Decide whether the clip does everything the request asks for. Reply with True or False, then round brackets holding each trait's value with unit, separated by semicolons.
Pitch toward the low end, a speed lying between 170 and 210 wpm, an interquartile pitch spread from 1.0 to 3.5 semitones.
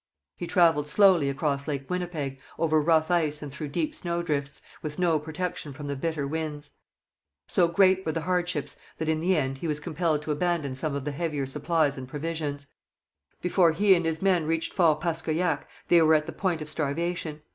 False (160 Hz; 190 wpm; 2.6 semitones)